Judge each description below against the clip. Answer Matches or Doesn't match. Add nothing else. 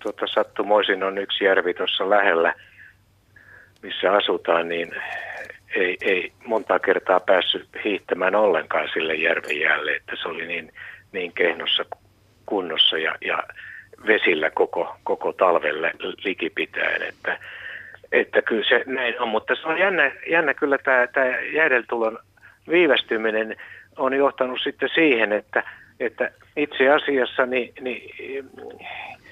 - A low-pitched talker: Doesn't match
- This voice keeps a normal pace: Matches